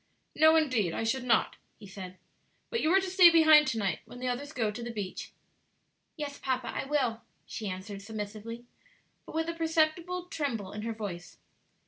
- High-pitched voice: Yes, high, 245 Hz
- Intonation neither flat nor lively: No, wide, 6.8 semitones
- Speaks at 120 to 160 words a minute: No, average, 185 wpm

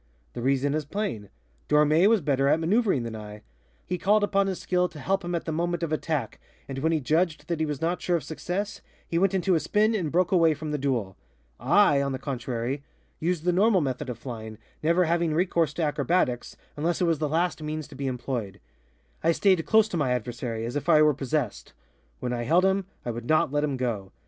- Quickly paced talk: Yes, fast, 225 wpm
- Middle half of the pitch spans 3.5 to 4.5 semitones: No, average, 5.1 semitones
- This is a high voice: No, medium, 155 Hz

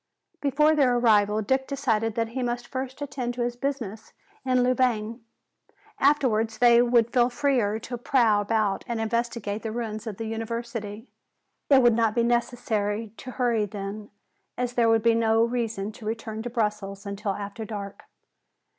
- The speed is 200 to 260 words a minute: No, average, 165 wpm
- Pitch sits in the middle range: No, high, 230 Hz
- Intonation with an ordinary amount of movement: No, narrow, 2.3 semitones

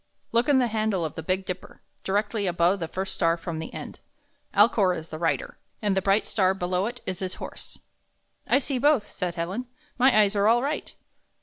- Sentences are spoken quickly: Yes, fast, 210 wpm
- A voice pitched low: No, high, 195 Hz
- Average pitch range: Yes, average, 3.9 semitones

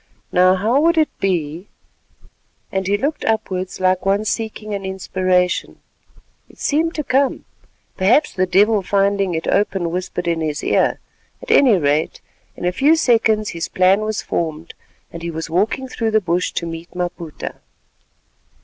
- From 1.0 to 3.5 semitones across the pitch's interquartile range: No, average, 3.9 semitones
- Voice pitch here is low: No, high, 190 Hz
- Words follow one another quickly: No, average, 155 wpm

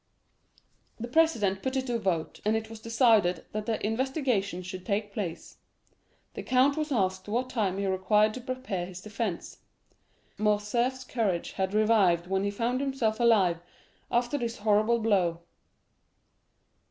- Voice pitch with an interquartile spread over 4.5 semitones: No, average, 4.0 semitones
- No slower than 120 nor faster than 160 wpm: Yes, average, 150 wpm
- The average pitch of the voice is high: Yes, high, 215 Hz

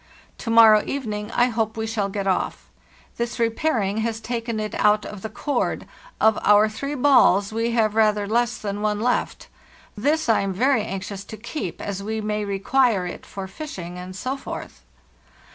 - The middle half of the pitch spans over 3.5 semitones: No, narrow, 2.5 semitones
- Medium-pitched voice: No, high, 215 Hz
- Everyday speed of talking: Yes, average, 175 wpm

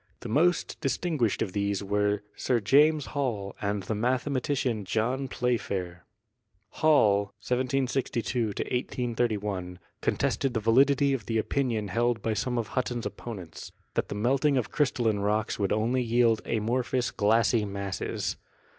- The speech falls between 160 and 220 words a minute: No, average, 145 wpm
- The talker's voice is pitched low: Yes, low, 115 Hz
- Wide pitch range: No, average, 3.9 semitones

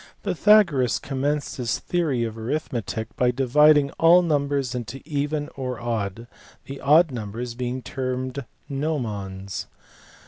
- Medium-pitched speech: No, low, 130 Hz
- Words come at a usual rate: No, slow, 115 wpm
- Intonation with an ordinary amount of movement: Yes, average, 3.7 semitones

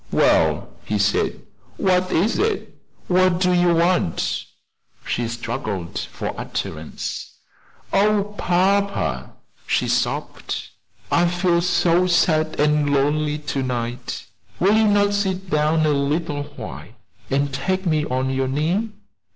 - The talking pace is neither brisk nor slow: No, slow, 125 wpm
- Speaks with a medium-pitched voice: Yes, medium, 165 Hz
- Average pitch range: Yes, average, 4.8 semitones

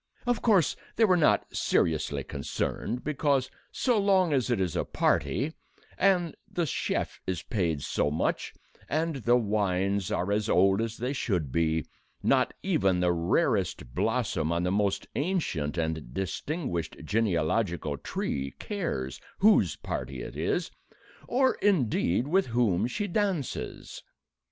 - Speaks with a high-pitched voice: No, low, 105 Hz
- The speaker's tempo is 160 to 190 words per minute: No, slow, 135 wpm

